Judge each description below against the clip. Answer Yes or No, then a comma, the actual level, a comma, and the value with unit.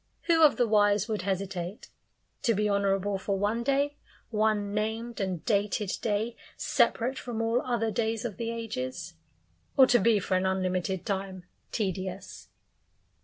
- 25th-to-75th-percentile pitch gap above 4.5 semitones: No, average, 3.2 semitones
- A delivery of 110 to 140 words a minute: No, average, 150 wpm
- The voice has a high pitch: Yes, high, 210 Hz